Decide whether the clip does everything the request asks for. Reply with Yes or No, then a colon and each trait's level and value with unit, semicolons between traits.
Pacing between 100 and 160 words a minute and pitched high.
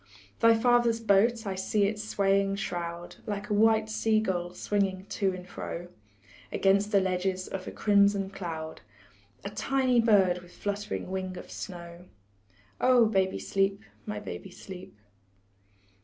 Yes: average, 140 wpm; high, 200 Hz